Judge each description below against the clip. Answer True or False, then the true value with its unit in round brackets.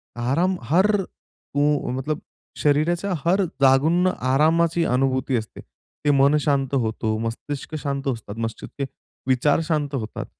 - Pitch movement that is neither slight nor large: True (3.5 semitones)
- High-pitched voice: False (140 Hz)